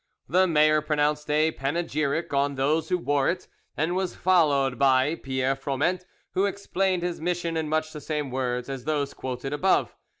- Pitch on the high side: No, medium, 150 Hz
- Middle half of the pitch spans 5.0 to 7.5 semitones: No, average, 3.8 semitones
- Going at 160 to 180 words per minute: Yes, average, 170 wpm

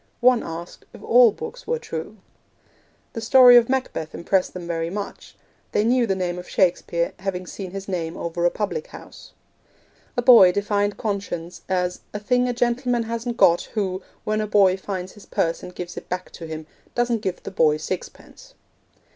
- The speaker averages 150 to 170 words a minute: No, average, 180 wpm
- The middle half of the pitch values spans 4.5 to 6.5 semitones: Yes, average, 4.9 semitones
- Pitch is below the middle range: No, high, 200 Hz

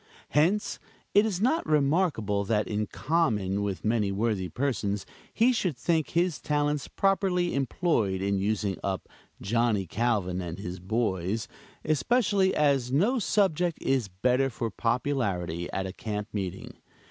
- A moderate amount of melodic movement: No, wide, 8.5 semitones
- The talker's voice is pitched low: Yes, low, 120 Hz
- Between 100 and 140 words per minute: Yes, slow, 135 wpm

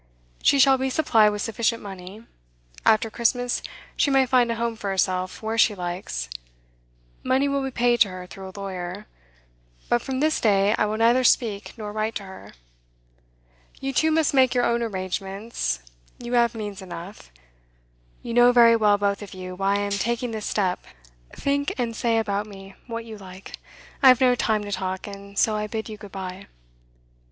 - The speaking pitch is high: Yes, high, 215 Hz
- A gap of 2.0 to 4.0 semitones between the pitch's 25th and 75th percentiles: Yes, average, 3.5 semitones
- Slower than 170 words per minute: No, average, 185 wpm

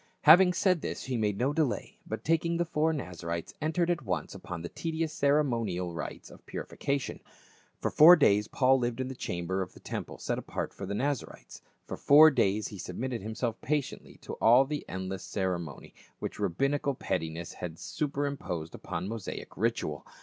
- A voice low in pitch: Yes, low, 120 Hz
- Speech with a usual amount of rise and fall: No, wide, 7.9 semitones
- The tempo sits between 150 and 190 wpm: Yes, average, 180 wpm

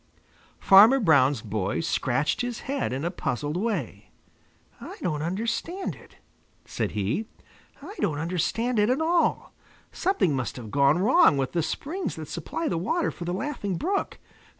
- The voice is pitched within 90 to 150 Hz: No, medium, 180 Hz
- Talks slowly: No, average, 155 wpm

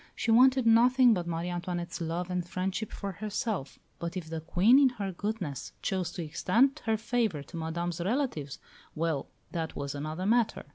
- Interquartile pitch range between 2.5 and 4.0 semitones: No, average, 5.2 semitones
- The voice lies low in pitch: No, medium, 185 Hz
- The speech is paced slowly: No, average, 175 wpm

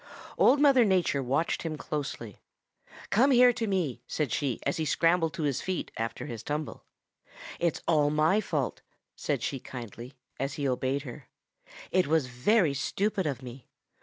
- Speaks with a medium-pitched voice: Yes, medium, 150 Hz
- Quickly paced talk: No, average, 165 wpm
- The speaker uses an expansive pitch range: Yes, wide, 5.9 semitones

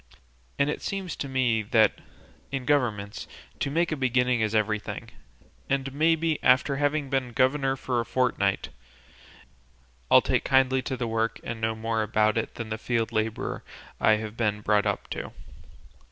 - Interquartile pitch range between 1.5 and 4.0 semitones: Yes, average, 3.6 semitones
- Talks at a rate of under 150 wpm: No, average, 160 wpm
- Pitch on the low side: Yes, low, 125 Hz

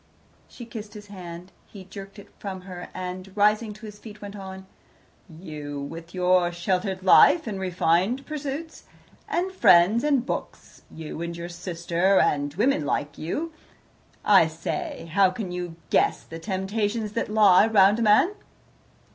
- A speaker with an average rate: Yes, average, 155 wpm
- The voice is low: No, high, 190 Hz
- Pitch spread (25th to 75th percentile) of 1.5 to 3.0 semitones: No, average, 3.5 semitones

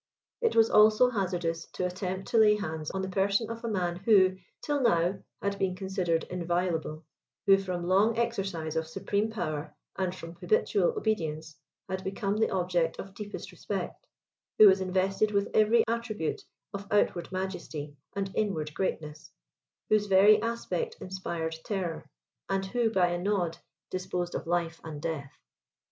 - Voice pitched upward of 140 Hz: Yes, high, 190 Hz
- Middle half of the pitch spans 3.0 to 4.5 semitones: Yes, average, 3.5 semitones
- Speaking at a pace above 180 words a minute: No, average, 155 wpm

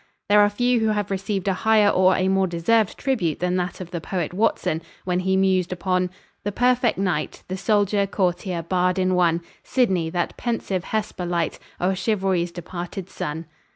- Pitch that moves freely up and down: No, narrow, 2.6 semitones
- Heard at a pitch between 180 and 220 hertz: Yes, medium, 185 Hz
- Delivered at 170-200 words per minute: Yes, average, 180 wpm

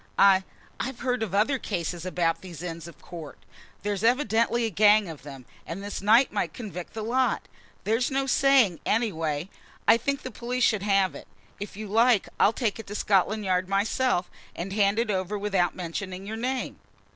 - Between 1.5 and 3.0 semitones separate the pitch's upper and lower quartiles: No, average, 4.0 semitones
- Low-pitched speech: No, high, 205 Hz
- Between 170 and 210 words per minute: Yes, average, 185 wpm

